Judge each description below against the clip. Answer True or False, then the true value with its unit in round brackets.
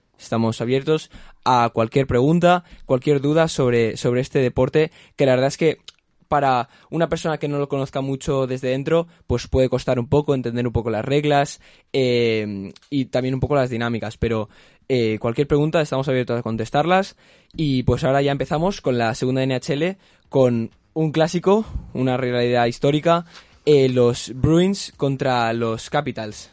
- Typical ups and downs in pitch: True (3.7 semitones)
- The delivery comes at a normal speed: True (165 wpm)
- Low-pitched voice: True (130 Hz)